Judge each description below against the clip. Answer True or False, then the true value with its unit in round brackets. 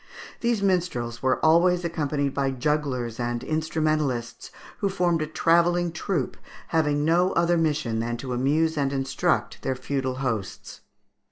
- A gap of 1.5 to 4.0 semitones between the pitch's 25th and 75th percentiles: False (4.4 semitones)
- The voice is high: False (150 Hz)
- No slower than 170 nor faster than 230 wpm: False (150 wpm)